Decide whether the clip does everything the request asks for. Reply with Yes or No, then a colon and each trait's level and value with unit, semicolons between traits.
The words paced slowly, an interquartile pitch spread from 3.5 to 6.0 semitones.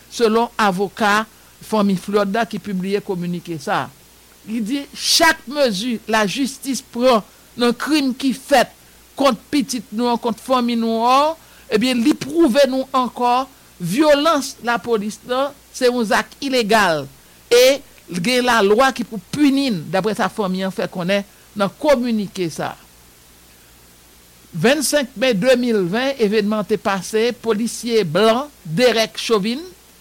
Yes: slow, 130 wpm; average, 4.6 semitones